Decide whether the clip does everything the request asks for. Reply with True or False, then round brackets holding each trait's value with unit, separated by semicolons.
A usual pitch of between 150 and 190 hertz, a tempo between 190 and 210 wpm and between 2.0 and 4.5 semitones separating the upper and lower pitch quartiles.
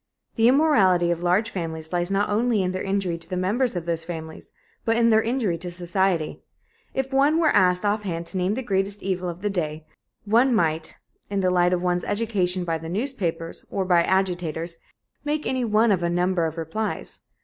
True (185 Hz; 200 wpm; 4.0 semitones)